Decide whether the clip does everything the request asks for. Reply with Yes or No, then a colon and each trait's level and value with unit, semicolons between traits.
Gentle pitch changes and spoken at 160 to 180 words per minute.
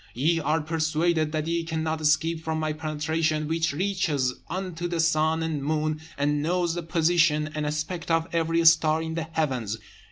Yes: narrow, 1.4 semitones; average, 170 wpm